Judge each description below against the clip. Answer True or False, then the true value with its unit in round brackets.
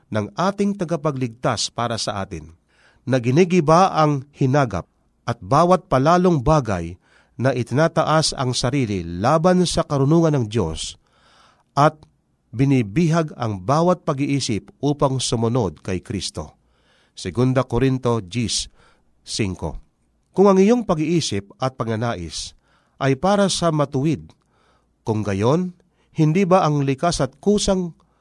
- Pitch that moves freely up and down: True (7.0 semitones)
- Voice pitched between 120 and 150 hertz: True (135 Hz)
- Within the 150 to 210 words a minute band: False (115 wpm)